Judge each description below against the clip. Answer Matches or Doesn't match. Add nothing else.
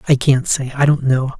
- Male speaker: Matches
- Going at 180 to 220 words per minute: Doesn't match